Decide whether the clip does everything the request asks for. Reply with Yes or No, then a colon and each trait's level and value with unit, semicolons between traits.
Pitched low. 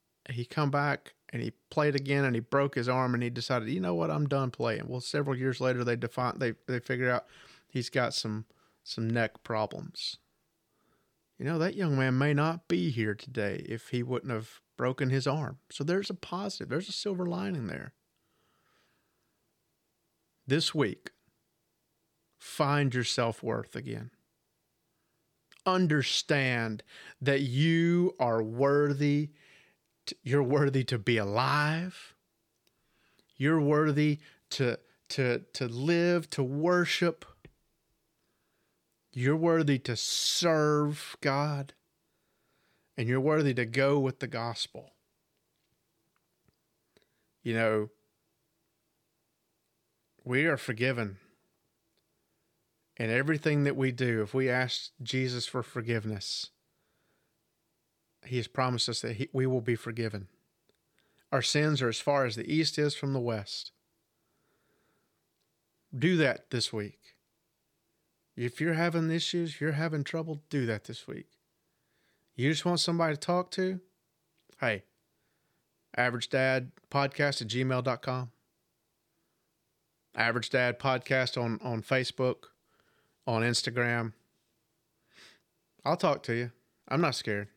Yes: low, 130 Hz